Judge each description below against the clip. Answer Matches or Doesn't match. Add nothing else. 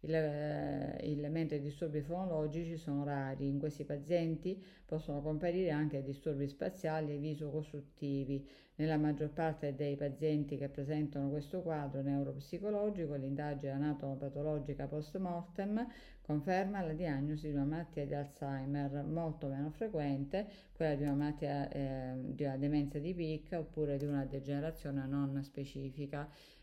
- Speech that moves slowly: Doesn't match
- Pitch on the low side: Doesn't match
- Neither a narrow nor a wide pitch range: Doesn't match